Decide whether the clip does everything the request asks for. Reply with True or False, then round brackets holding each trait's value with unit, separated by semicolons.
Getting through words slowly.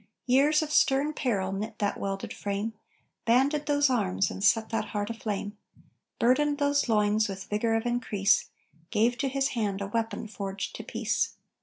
False (165 wpm)